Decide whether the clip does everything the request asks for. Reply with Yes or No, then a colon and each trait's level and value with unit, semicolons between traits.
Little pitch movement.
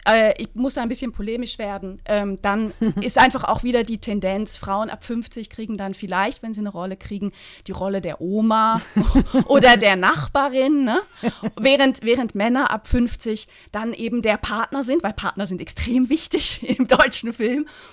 No: average, 3.7 semitones